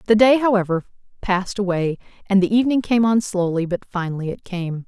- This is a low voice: No, high, 200 Hz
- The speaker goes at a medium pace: Yes, average, 185 wpm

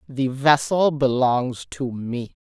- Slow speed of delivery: Yes, slow, 125 wpm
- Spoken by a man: No, female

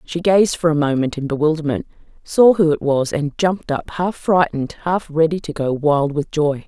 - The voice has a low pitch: No, medium, 155 Hz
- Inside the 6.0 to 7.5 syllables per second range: No, 5.1 syllables/s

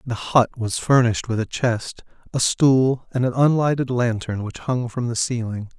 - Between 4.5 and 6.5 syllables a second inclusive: Yes, 4.6 syllables/s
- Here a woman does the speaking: No, male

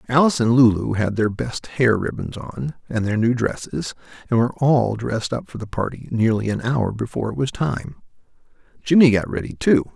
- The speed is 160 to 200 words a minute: Yes, average, 195 wpm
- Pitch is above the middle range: No, low, 115 Hz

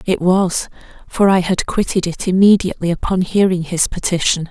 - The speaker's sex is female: Yes, female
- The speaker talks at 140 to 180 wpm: Yes, average, 160 wpm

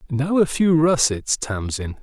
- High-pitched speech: No, medium, 140 Hz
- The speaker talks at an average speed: Yes, average, 150 wpm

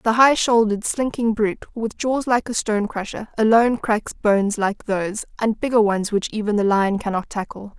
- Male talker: No, female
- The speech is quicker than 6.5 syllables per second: No, 5.3 syllables/s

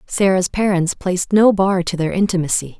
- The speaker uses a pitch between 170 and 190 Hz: Yes, medium, 185 Hz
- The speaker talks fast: No, average, 170 wpm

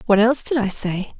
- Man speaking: No, female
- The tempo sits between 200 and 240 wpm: No, fast, 250 wpm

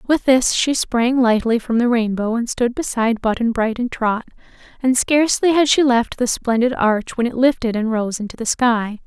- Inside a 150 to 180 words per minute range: No, fast, 205 wpm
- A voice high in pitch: Yes, high, 240 Hz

